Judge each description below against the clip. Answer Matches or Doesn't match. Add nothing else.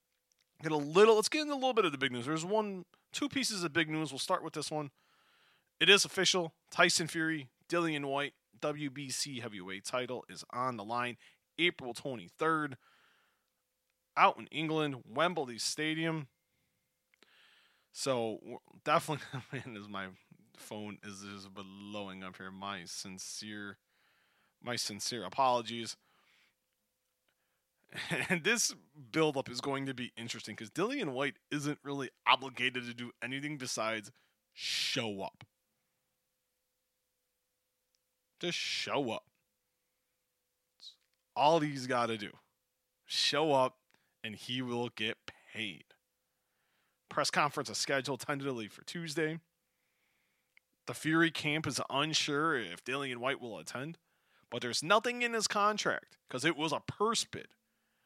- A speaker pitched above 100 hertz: Matches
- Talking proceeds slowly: Matches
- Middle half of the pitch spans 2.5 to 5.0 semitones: Doesn't match